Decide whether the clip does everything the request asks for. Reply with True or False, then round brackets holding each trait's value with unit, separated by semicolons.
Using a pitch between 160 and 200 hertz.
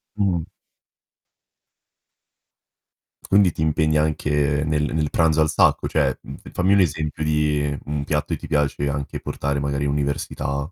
False (75 Hz)